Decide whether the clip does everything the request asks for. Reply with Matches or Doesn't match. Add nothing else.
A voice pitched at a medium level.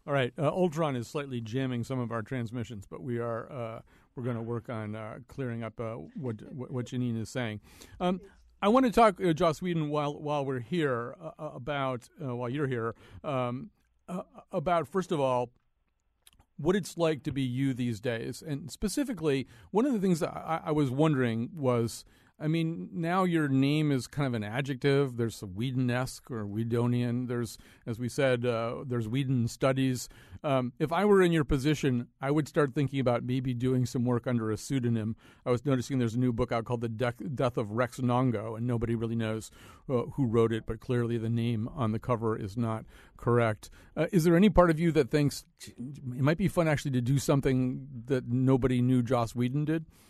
Doesn't match